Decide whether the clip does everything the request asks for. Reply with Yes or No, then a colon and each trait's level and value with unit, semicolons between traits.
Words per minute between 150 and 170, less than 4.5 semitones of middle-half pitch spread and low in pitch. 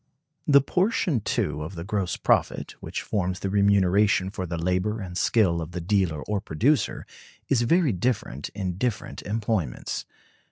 Yes: average, 155 wpm; average, 4.1 semitones; low, 100 Hz